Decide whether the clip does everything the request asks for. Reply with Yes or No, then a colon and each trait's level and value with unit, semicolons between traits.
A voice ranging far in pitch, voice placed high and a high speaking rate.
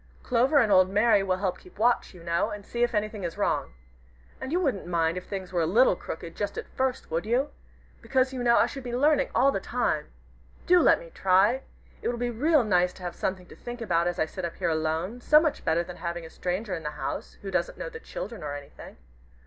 Yes: wide, 6.1 semitones; high, 205 Hz; fast, 240 wpm